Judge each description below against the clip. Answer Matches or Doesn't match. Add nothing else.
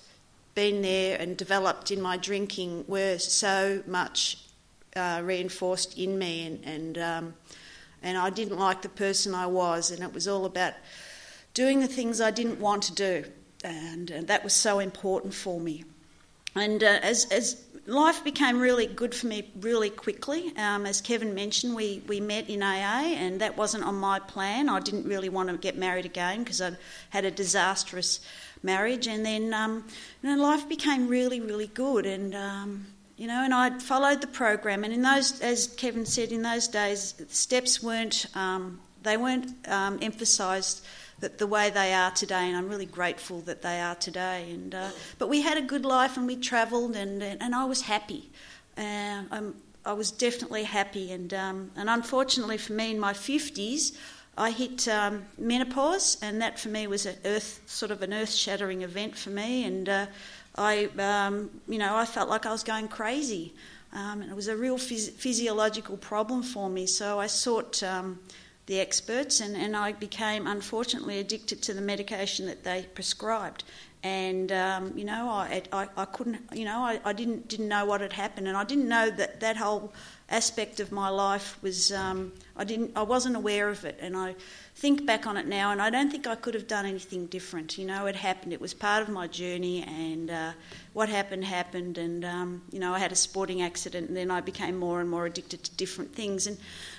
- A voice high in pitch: Matches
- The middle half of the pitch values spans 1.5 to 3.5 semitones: Matches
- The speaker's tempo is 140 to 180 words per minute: Doesn't match